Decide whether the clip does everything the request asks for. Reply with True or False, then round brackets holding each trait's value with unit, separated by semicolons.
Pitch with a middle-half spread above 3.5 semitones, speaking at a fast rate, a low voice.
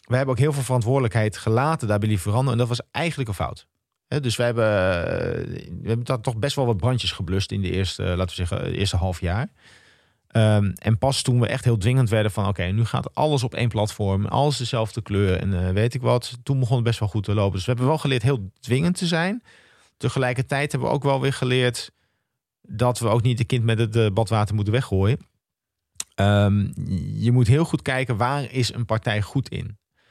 True (3.9 semitones; 215 wpm; 120 Hz)